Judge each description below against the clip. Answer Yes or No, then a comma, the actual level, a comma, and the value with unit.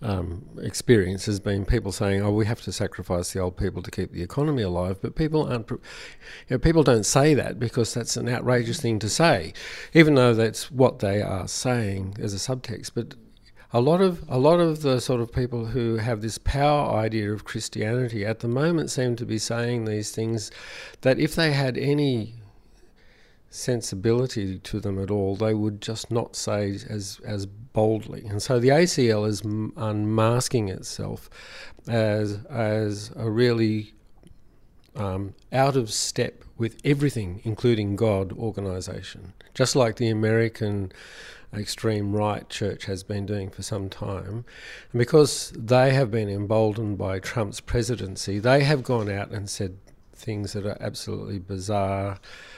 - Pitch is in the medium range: No, low, 110 Hz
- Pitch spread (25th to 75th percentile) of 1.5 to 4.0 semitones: Yes, average, 3.5 semitones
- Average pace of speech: Yes, average, 170 wpm